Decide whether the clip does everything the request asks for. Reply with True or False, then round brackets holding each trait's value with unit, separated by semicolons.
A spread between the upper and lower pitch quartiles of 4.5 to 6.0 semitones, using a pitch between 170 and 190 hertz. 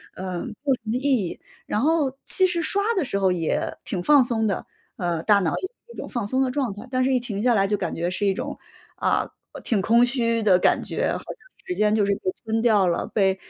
False (5.0 semitones; 225 Hz)